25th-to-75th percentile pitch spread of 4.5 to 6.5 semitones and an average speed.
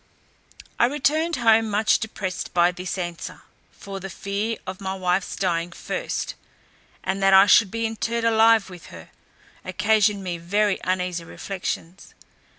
No: average, 3.3 semitones; average, 145 wpm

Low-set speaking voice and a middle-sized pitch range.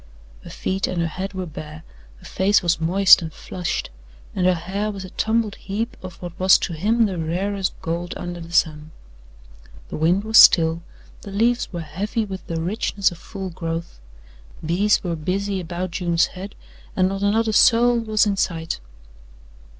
No: medium, 185 Hz; average, 3.3 semitones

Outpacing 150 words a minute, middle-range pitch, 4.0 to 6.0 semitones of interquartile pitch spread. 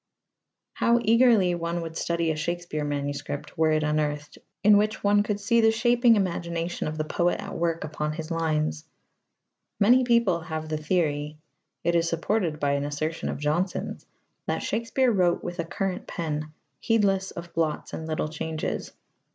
Yes: average, 165 wpm; medium, 170 Hz; average, 4.7 semitones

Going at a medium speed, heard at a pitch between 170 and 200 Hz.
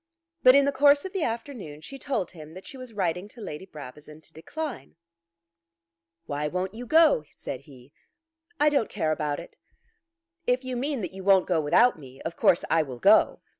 Yes: average, 195 wpm; high, 190 Hz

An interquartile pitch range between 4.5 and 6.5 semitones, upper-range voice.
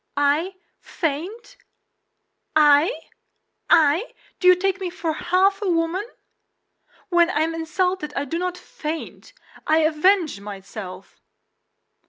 No: average, 3.7 semitones; very high, 330 Hz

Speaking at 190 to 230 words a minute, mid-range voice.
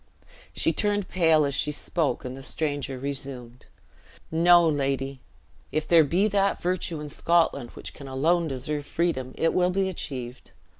No: average, 155 wpm; medium, 150 Hz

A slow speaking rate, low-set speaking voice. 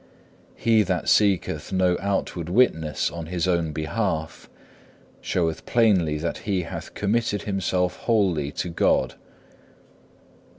Yes: slow, 120 wpm; very low, 90 Hz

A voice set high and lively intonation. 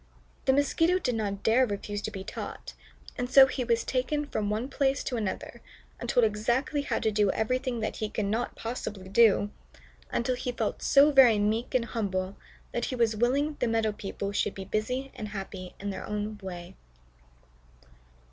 No: high, 225 Hz; average, 3.7 semitones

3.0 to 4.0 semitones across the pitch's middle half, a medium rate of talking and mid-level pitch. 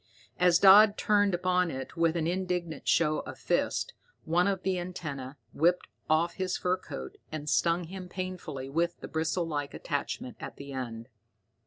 Yes: average, 3.6 semitones; average, 165 wpm; medium, 170 Hz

